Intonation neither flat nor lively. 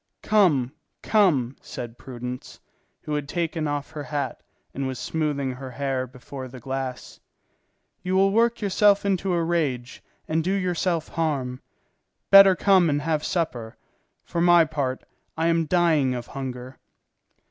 Yes: average, 5.0 semitones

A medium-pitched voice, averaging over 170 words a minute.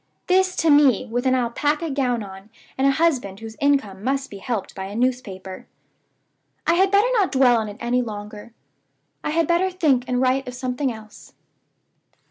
No: very high, 255 Hz; average, 180 wpm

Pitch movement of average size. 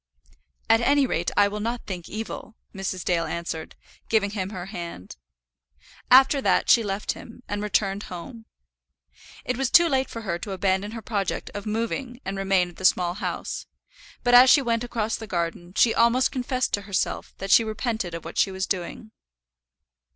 Yes: average, 3.8 semitones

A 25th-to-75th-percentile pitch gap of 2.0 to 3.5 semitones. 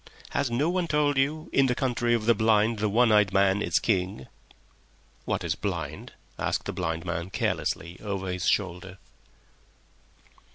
No: average, 4.7 semitones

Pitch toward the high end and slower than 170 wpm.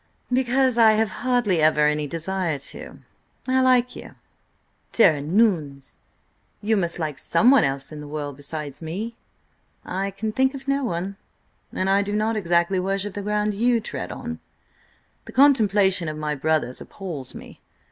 Yes: high, 195 Hz; average, 160 wpm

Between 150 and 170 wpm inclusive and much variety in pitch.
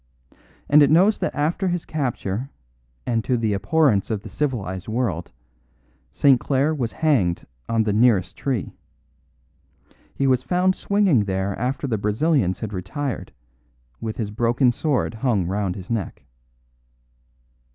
No: average, 140 wpm; wide, 5.9 semitones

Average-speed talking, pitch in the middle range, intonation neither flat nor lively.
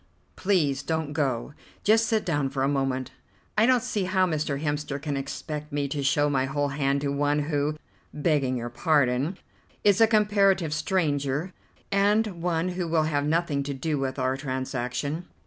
Yes: average, 170 wpm; medium, 150 Hz; average, 4.1 semitones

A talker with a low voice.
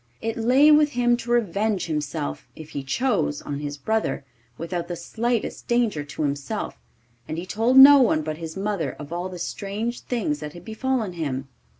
No: medium, 185 Hz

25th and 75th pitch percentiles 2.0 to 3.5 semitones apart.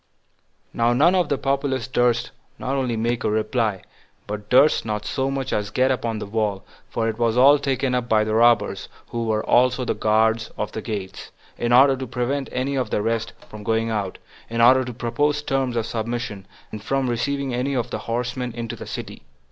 Yes: average, 2.9 semitones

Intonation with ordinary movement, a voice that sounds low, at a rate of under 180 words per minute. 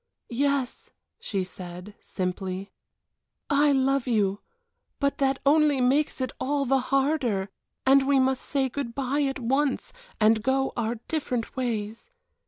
No: average, 3.9 semitones; very high, 260 Hz; slow, 135 wpm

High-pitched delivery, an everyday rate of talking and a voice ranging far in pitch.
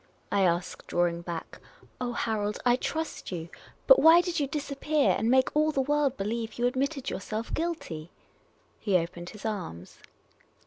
Yes: high, 240 Hz; average, 165 wpm; wide, 8.1 semitones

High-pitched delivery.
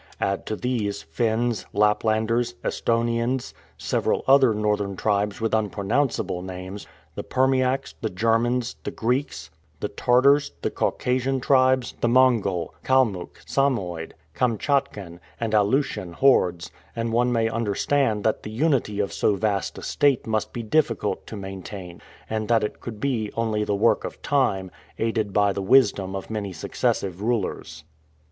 No: low, 110 Hz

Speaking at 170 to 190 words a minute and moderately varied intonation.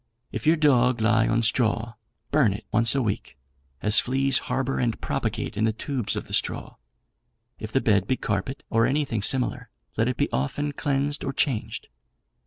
Yes: average, 180 wpm; average, 3.8 semitones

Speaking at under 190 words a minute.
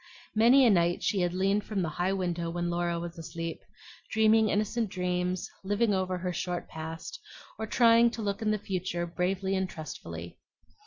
Yes: average, 175 wpm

